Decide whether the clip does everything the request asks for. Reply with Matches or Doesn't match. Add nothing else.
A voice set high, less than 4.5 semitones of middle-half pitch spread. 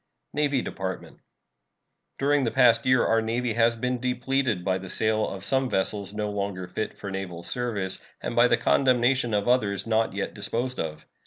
Doesn't match